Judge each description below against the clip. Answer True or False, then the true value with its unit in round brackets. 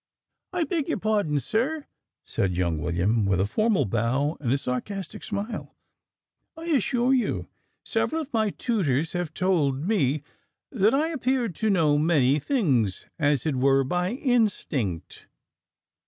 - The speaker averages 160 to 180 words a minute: False (140 wpm)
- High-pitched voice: False (175 Hz)